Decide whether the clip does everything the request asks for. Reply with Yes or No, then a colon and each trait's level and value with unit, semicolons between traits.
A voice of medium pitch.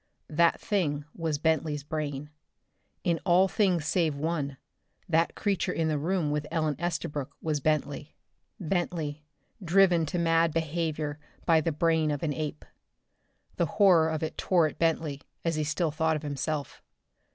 Yes: medium, 160 Hz